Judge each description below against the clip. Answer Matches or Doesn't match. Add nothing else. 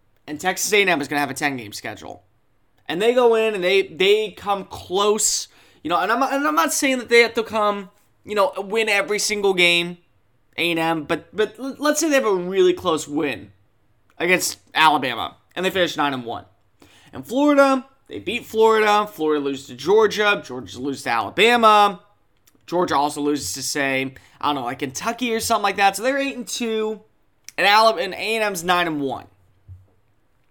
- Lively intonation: Matches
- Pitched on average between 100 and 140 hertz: Doesn't match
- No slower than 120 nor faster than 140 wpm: Doesn't match